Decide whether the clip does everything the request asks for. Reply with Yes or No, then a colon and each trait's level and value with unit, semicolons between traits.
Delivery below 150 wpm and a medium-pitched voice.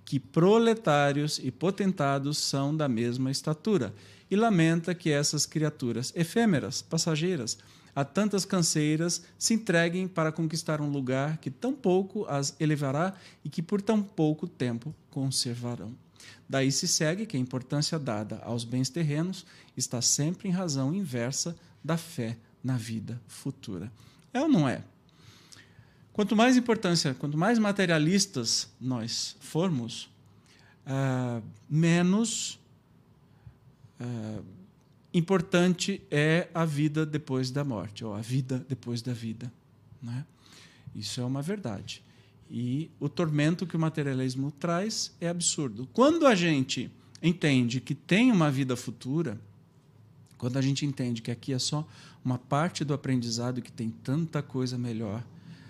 Yes: average, 130 wpm; medium, 145 Hz